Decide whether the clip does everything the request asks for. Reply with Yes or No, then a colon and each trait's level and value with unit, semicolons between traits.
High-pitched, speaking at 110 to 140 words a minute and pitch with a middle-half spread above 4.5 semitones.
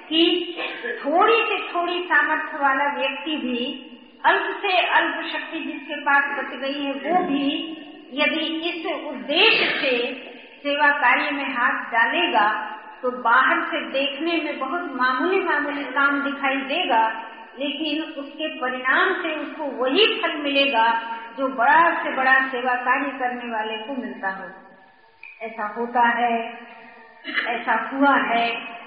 No: very high, 280 Hz; average, 135 wpm; average, 4.2 semitones